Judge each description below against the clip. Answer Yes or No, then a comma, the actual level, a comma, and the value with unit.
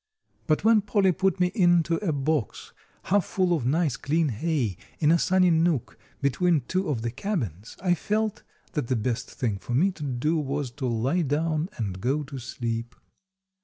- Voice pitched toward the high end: No, medium, 155 Hz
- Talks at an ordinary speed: Yes, average, 180 wpm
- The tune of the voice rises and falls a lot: Yes, wide, 6.0 semitones